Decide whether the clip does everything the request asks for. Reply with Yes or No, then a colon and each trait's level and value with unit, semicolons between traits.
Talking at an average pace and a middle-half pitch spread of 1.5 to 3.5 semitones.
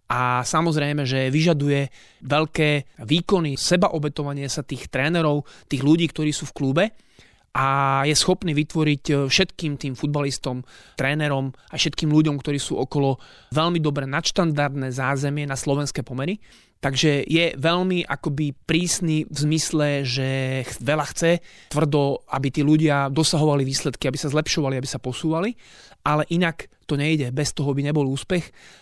Yes: average, 140 wpm; narrow, 2.4 semitones